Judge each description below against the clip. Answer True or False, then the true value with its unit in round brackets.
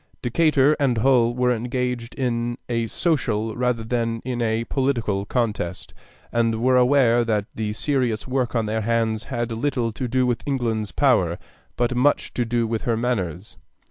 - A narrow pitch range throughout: True (2.1 semitones)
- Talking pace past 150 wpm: True (165 wpm)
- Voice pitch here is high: False (120 Hz)